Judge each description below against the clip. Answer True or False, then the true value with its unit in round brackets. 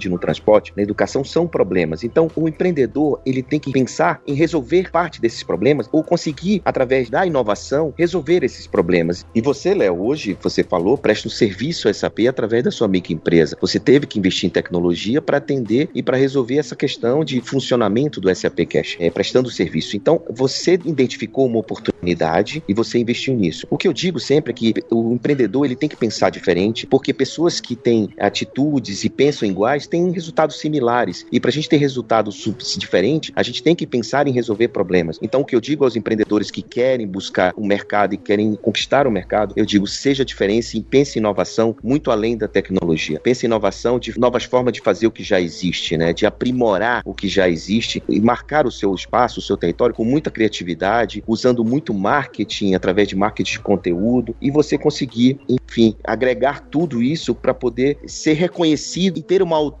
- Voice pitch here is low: True (120 Hz)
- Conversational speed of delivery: False (195 wpm)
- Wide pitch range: True (5.7 semitones)